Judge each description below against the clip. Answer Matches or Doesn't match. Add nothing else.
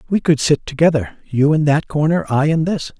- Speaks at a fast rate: Matches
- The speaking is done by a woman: Doesn't match